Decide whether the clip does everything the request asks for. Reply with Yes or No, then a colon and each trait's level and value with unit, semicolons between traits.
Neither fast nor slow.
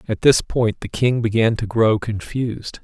Yes: average, 190 wpm